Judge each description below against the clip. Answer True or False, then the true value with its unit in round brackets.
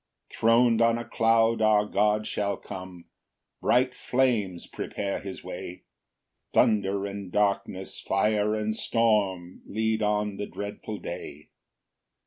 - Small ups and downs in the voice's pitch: True (2.2 semitones)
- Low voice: True (105 Hz)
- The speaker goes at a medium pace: False (120 wpm)